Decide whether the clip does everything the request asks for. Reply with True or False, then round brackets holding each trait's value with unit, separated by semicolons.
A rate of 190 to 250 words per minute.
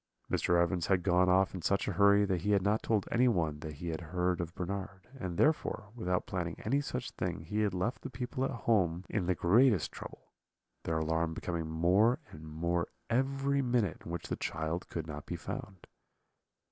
True (195 wpm)